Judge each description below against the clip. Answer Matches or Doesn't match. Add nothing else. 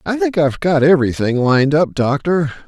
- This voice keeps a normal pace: Matches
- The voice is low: Doesn't match